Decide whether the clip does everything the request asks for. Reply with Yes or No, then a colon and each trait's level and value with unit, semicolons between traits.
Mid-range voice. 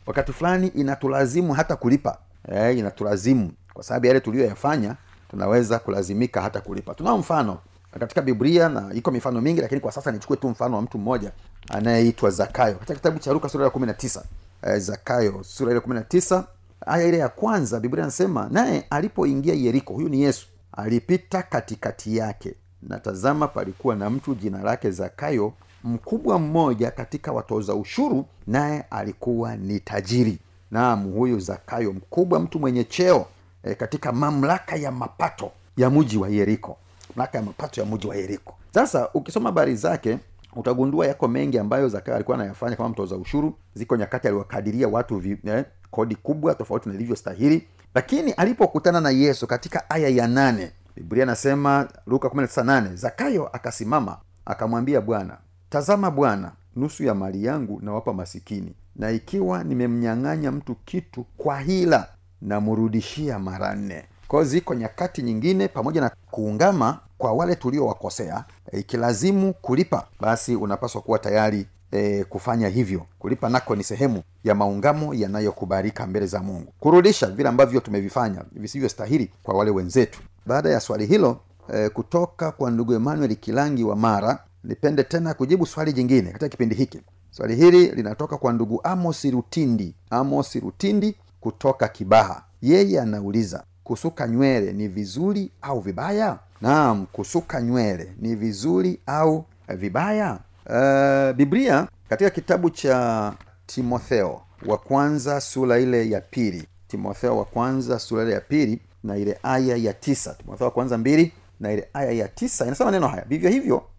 No: low, 120 Hz